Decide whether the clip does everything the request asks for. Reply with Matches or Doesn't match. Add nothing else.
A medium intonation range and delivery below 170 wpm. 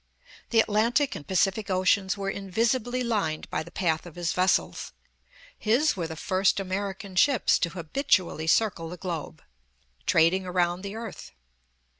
Matches